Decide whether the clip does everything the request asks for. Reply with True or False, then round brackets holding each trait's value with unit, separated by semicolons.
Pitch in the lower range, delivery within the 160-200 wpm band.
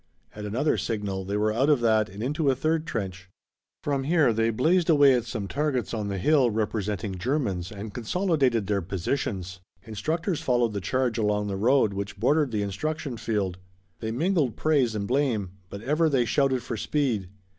True (115 Hz; 180 wpm)